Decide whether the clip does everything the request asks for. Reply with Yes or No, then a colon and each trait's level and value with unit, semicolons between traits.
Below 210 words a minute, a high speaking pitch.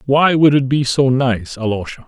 No: average, 200 wpm; low, 130 Hz